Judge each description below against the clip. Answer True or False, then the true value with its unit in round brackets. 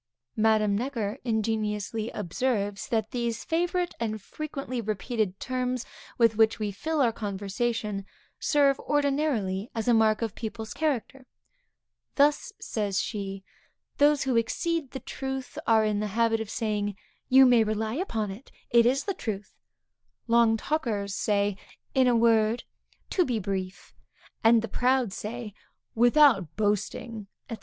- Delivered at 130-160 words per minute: True (140 wpm)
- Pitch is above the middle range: True (225 Hz)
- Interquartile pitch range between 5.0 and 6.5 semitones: False (3.5 semitones)